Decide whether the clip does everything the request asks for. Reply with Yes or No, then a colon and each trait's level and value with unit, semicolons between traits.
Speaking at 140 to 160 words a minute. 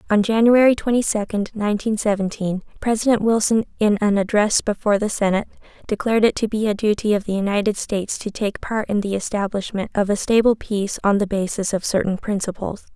No: average, 185 wpm